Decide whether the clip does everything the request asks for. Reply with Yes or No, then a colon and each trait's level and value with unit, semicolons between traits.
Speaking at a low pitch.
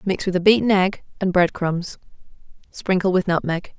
No: medium, 185 Hz